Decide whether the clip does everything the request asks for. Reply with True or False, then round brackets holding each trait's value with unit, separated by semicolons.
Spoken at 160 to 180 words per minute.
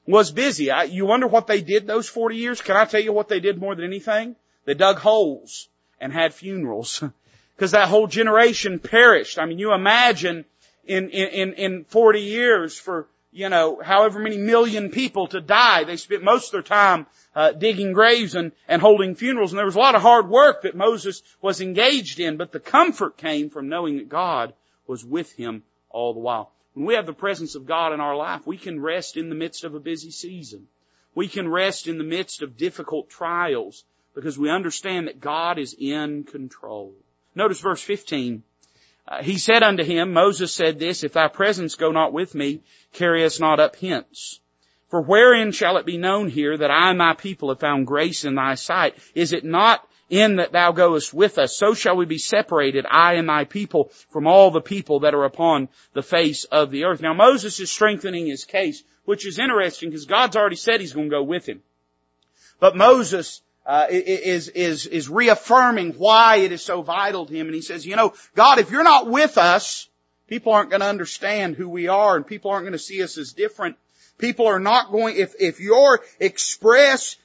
False (205 wpm)